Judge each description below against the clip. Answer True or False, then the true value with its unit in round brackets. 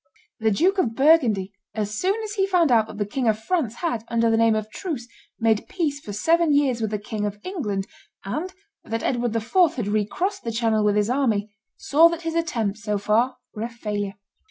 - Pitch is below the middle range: False (230 Hz)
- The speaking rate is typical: False (210 wpm)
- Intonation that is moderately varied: False (7.2 semitones)